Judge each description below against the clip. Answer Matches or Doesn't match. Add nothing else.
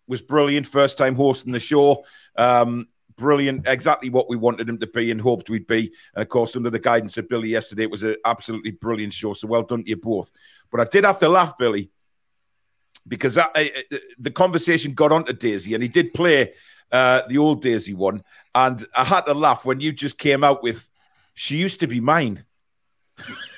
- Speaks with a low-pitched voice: Matches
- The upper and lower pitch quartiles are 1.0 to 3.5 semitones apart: Doesn't match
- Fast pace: Matches